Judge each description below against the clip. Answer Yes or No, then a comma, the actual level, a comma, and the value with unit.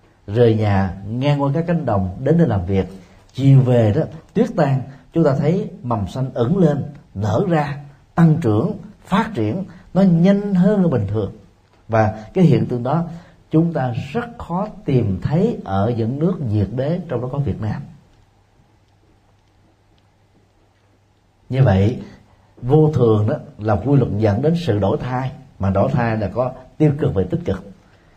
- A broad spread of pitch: Yes, wide, 7.1 semitones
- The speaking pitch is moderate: No, low, 125 Hz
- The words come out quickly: No, slow, 165 wpm